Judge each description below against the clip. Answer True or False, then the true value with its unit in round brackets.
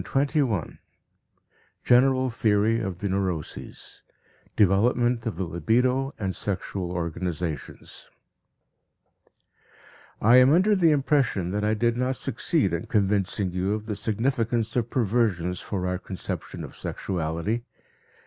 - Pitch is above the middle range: False (105 Hz)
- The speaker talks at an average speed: False (125 wpm)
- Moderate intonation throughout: True (5.0 semitones)